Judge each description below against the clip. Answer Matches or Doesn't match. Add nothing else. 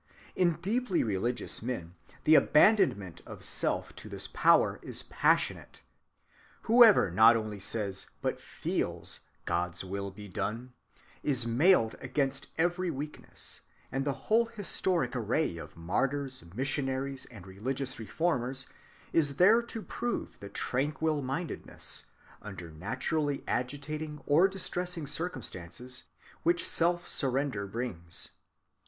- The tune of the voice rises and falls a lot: Matches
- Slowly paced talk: Matches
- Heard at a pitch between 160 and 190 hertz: Doesn't match